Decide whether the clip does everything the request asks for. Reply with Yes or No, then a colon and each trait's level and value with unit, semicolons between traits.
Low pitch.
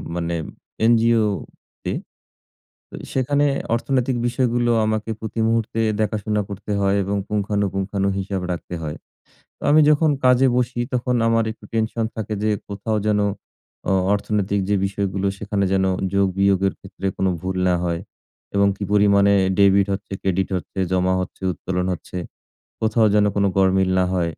Yes: low, 100 Hz